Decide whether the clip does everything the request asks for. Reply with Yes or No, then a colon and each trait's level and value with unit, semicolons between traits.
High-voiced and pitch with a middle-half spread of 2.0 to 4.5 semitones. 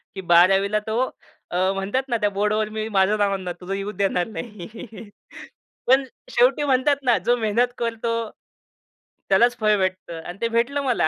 Yes: high, 215 Hz; average, 3.6 semitones